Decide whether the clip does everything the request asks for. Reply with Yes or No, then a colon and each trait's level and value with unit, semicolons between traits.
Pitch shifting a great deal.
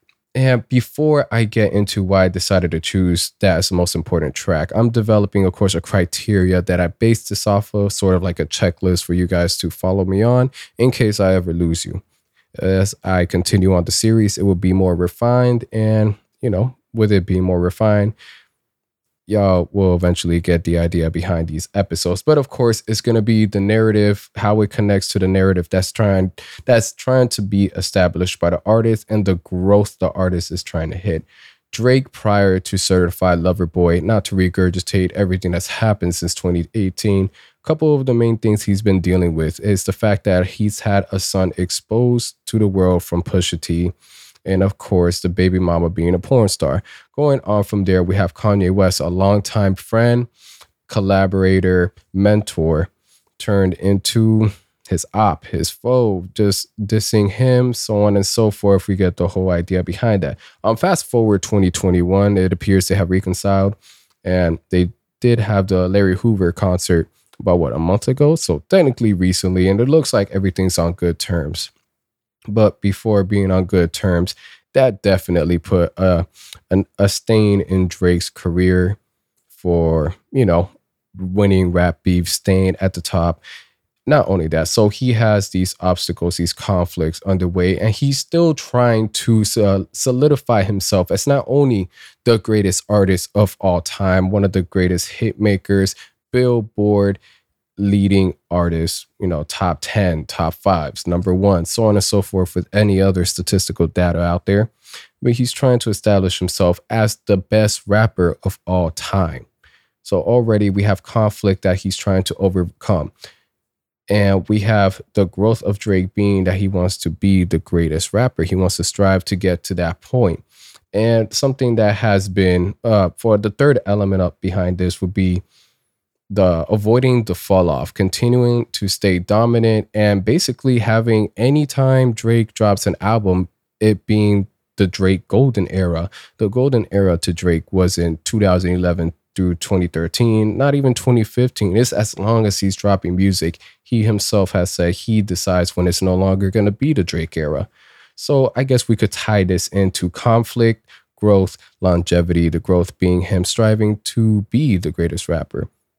No: average, 3.1 semitones